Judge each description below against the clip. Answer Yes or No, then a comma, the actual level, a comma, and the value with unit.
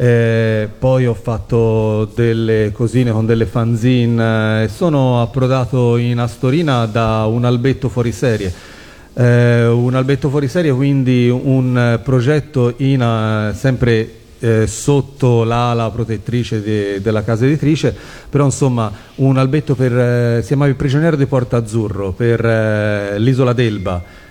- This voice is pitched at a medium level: No, low, 120 Hz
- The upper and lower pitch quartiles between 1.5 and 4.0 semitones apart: Yes, average, 2.7 semitones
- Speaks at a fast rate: No, average, 135 wpm